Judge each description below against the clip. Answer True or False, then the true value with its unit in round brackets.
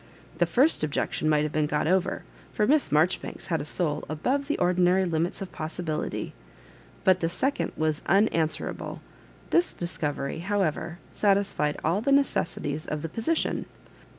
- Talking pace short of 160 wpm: True (150 wpm)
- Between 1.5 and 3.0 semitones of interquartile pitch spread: False (4.6 semitones)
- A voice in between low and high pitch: True (175 Hz)